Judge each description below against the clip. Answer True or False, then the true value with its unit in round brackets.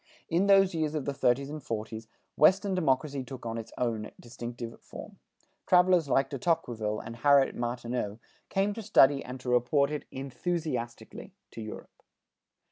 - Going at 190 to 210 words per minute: False (150 wpm)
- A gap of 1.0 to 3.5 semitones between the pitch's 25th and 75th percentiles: False (5.3 semitones)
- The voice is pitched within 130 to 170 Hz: True (135 Hz)